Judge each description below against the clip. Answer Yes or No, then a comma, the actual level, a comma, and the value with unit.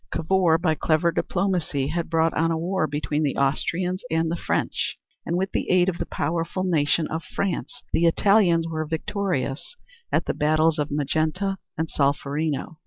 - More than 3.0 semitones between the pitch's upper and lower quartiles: No, narrow, 2.5 semitones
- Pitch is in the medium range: Yes, medium, 165 Hz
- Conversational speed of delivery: Yes, average, 170 wpm